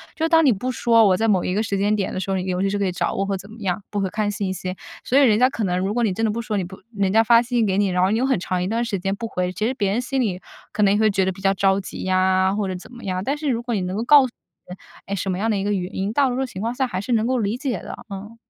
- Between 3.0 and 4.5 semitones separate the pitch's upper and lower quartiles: Yes, average, 3.5 semitones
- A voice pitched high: Yes, high, 205 Hz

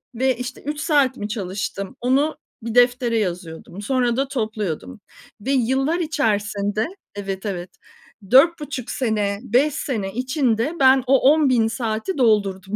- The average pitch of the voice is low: No, high, 240 Hz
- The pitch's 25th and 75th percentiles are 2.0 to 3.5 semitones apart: No, average, 4.5 semitones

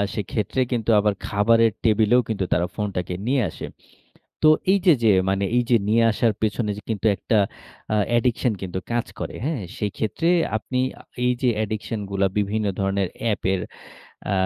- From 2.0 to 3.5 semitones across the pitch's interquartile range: Yes, average, 2.7 semitones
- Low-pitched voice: Yes, low, 110 Hz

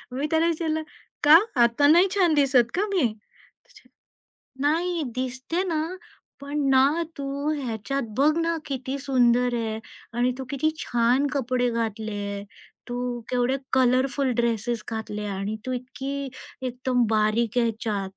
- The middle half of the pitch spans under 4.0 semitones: Yes, average, 3.6 semitones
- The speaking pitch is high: Yes, very high, 255 Hz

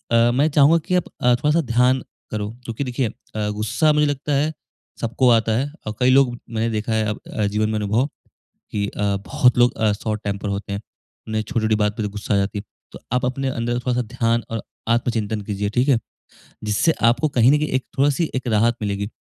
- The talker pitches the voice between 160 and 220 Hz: No, low, 115 Hz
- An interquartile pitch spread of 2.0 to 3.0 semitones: No, average, 3.4 semitones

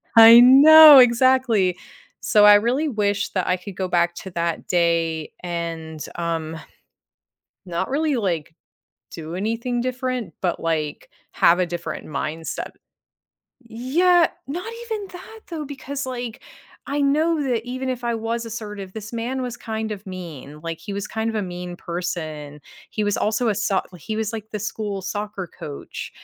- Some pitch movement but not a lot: No, wide, 6.4 semitones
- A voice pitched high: Yes, high, 215 Hz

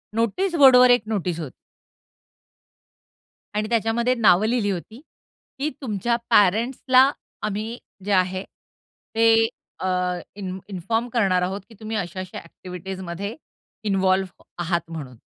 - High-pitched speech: Yes, high, 205 Hz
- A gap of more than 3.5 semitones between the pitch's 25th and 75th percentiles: Yes, average, 3.9 semitones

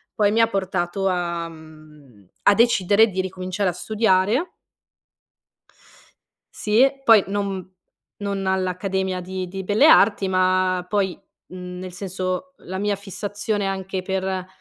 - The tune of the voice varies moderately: No, narrow, 1.8 semitones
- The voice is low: No, high, 190 Hz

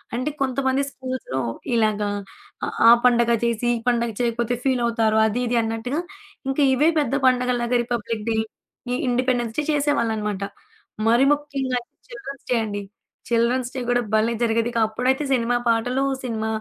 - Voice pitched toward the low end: No, high, 240 Hz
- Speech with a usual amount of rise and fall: No, narrow, 2.2 semitones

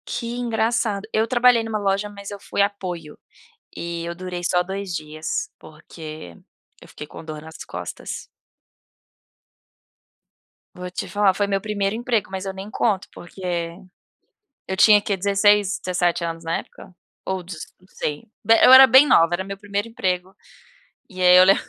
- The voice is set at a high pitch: Yes, high, 195 Hz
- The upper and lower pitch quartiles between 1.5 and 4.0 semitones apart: Yes, average, 3.0 semitones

